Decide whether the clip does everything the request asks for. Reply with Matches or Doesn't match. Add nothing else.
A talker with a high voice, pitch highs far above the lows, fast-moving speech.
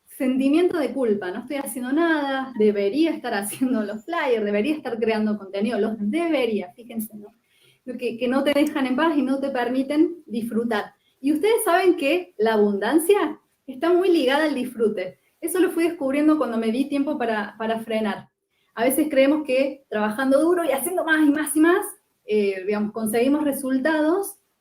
Doesn't match